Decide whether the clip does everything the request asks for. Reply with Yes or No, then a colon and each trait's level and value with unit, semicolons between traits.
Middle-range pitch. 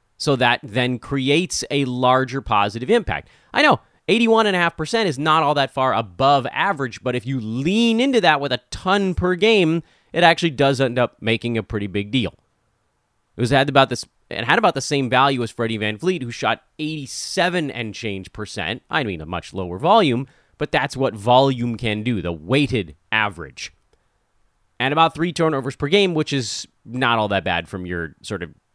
No: low, 130 Hz